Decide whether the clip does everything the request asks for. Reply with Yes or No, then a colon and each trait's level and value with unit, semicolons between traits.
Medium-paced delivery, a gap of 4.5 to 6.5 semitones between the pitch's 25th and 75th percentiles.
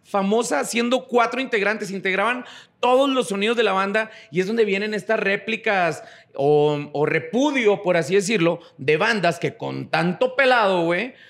Yes: average, 160 wpm; wide, 5.4 semitones